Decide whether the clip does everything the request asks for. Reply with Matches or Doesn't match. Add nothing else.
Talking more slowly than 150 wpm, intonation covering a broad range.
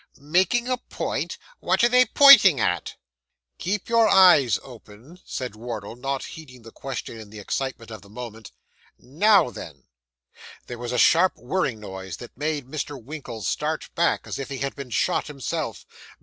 Doesn't match